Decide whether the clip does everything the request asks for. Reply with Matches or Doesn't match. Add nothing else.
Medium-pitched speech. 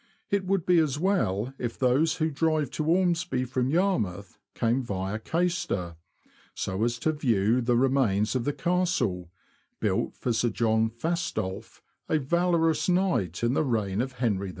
Doesn't match